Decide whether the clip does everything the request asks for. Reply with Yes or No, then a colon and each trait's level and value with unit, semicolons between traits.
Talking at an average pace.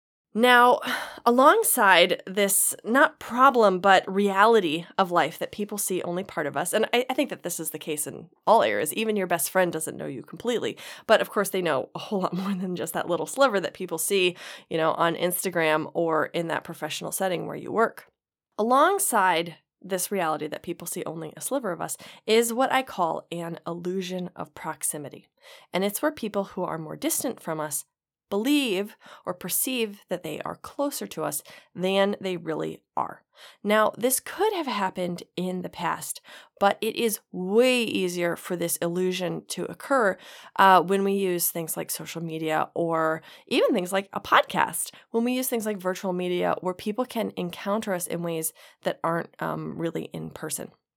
Yes: average, 185 wpm